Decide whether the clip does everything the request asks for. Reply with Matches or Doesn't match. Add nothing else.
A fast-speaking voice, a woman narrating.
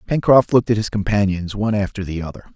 Doesn't match